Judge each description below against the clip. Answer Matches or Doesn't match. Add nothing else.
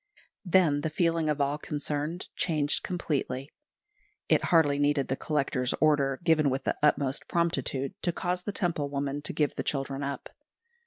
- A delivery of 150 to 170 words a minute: Matches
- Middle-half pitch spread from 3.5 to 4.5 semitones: Doesn't match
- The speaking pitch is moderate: Matches